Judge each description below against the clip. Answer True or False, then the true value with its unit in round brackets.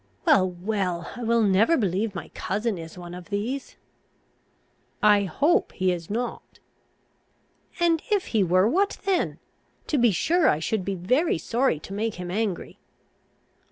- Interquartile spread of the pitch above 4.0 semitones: True (5.2 semitones)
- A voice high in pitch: True (205 Hz)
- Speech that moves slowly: False (155 wpm)